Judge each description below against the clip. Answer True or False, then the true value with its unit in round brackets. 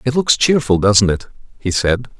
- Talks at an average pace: True (190 wpm)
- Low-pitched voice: True (115 Hz)